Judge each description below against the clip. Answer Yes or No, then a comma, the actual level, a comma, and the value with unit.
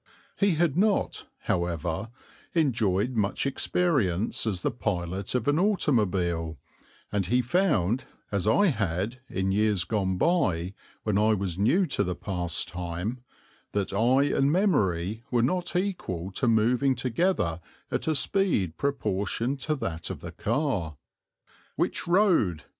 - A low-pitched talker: Yes, low, 110 Hz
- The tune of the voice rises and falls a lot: Yes, wide, 7.5 semitones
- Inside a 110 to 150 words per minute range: Yes, slow, 135 wpm